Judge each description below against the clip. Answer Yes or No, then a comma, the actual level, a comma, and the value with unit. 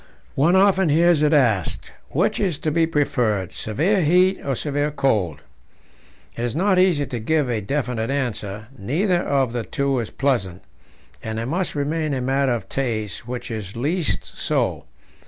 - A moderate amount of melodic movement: No, wide, 5.7 semitones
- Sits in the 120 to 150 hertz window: Yes, low, 135 Hz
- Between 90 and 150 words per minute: No, average, 165 wpm